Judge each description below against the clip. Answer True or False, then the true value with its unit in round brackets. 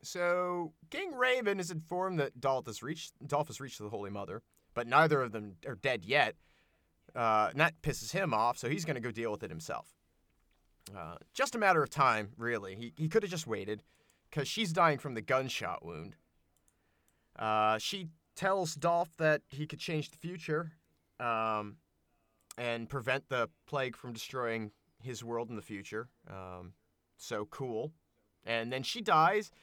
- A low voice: True (120 Hz)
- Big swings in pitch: True (7.3 semitones)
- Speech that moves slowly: False (175 wpm)